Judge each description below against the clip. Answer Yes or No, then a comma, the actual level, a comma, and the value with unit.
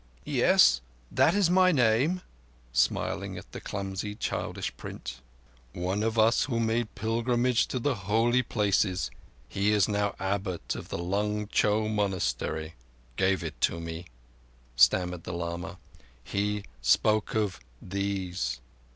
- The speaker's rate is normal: No, slow, 125 wpm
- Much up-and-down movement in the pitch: No, average, 4.1 semitones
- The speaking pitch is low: Yes, low, 100 Hz